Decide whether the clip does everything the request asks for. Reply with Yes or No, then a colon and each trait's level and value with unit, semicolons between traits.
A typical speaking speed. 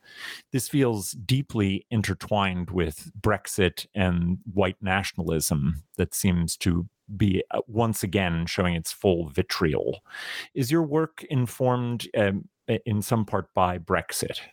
No: slow, 120 wpm